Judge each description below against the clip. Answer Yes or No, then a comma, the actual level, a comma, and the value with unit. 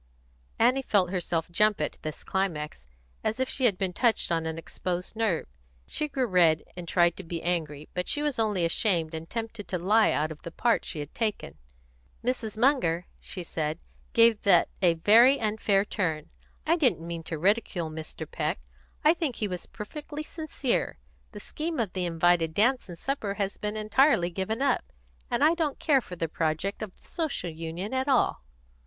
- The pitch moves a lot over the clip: Yes, wide, 6.1 semitones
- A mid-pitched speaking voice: No, high, 195 Hz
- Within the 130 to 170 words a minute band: No, average, 185 wpm